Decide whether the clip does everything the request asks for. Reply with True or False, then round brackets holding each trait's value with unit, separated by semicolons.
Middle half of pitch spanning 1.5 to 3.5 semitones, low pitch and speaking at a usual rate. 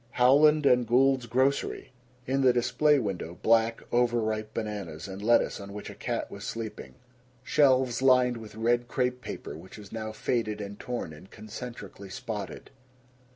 True (3.2 semitones; 115 Hz; 155 wpm)